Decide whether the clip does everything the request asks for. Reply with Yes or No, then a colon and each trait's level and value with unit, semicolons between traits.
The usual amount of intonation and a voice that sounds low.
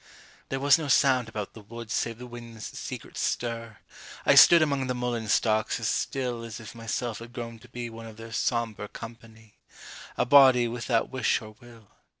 No: narrow, 1.7 semitones; low, 115 Hz